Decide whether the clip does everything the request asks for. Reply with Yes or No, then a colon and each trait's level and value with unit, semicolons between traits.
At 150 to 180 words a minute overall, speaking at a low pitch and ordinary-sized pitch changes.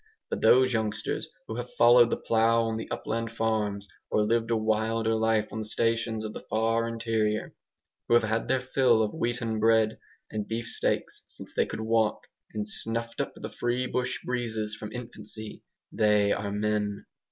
No: average, 175 wpm; low, 110 Hz; narrow, 1.3 semitones